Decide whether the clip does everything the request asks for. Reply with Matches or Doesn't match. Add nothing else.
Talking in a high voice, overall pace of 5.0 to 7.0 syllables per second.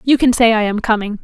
Matches